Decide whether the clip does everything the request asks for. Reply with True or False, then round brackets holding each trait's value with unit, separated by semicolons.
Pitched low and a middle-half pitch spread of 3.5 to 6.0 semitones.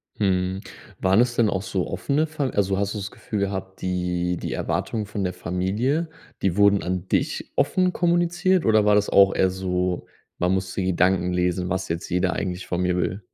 False (95 Hz; 2.4 semitones)